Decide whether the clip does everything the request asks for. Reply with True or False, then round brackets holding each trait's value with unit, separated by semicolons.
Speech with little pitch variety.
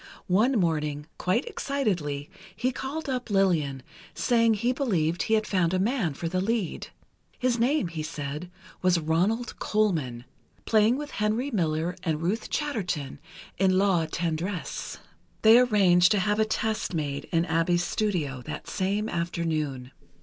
False (5.5 semitones)